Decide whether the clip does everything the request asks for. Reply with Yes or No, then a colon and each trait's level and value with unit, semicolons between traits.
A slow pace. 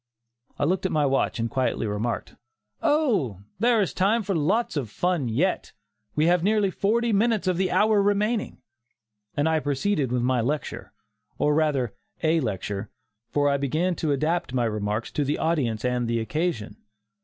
No: average, 170 wpm